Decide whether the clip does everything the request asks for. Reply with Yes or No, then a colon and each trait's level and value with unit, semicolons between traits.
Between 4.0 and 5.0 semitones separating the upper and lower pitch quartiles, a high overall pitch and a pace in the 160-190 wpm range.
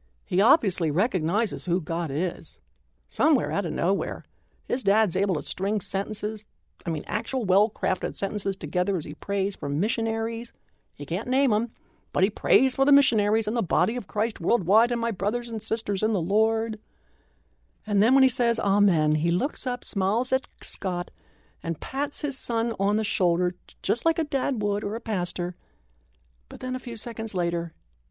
Yes: average, 4.6 semitones; high, 205 Hz; average, 180 wpm